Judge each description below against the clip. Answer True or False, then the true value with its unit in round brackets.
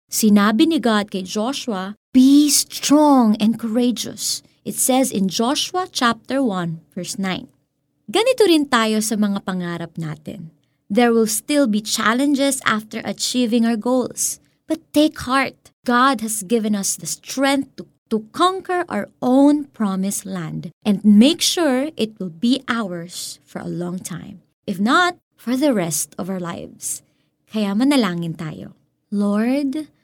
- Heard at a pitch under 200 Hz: False (220 Hz)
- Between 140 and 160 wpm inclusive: True (145 wpm)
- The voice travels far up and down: True (6.1 semitones)